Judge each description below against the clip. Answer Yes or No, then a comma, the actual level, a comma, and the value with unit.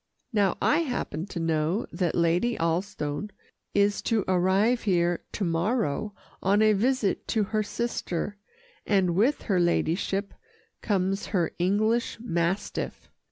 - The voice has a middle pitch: No, high, 195 Hz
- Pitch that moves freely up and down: No, average, 3.8 semitones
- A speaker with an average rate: No, slow, 125 wpm